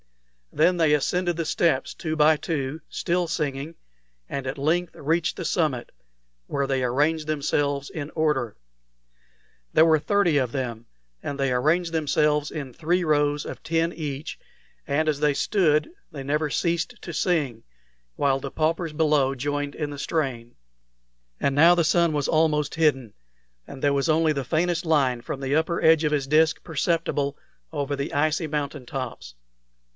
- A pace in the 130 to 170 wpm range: Yes, average, 160 wpm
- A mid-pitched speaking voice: Yes, medium, 150 Hz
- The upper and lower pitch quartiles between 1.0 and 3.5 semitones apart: Yes, average, 2.7 semitones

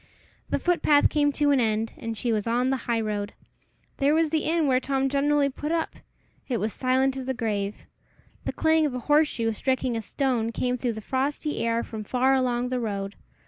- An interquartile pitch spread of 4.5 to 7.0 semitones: No, average, 4.0 semitones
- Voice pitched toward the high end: Yes, very high, 255 Hz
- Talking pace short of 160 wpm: No, fast, 205 wpm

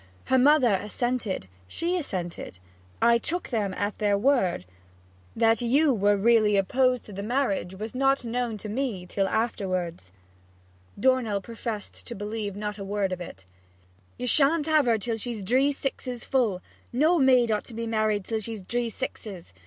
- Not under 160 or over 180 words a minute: Yes, average, 165 wpm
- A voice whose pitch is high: Yes, high, 225 Hz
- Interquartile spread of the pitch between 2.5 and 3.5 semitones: No, average, 3.9 semitones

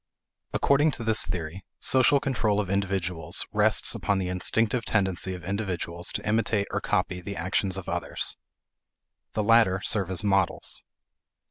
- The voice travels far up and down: No, average, 3.4 semitones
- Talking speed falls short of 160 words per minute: Yes, average, 145 wpm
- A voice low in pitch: Yes, low, 100 Hz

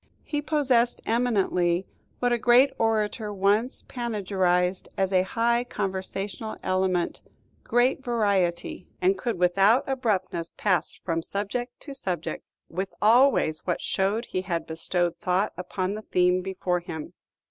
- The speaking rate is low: Yes, slow, 130 wpm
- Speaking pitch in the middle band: No, high, 195 Hz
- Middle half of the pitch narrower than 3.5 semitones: No, average, 4.6 semitones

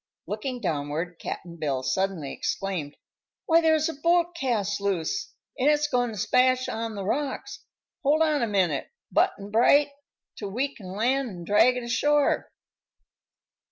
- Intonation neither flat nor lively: No, wide, 7.1 semitones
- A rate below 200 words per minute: Yes, average, 150 wpm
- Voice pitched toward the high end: Yes, high, 230 Hz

